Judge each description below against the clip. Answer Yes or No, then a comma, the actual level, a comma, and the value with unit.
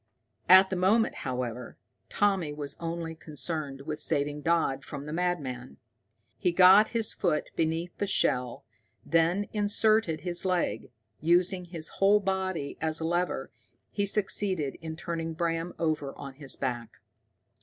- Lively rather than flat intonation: No, average, 4.1 semitones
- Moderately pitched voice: Yes, medium, 165 Hz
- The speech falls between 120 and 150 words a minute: Yes, average, 140 wpm